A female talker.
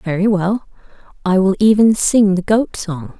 Yes: female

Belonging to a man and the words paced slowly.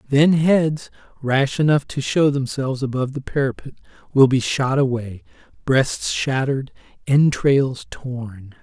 Yes: male; slow, 125 wpm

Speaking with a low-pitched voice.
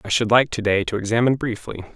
Yes: low, 115 Hz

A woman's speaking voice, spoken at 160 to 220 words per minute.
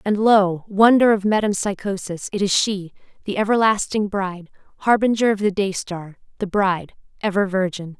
No: female; average, 145 wpm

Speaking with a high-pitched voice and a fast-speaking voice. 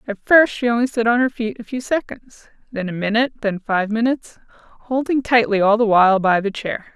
Yes: high, 225 Hz; fast, 215 wpm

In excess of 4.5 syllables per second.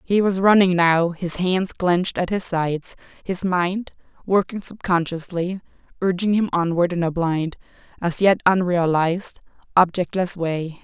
No: 4.4 syllables/s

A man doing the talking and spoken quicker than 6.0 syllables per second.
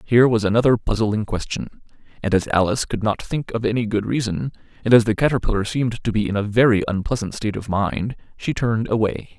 Yes: male; 6.2 syllables/s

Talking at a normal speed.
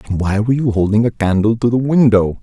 No: fast, 245 wpm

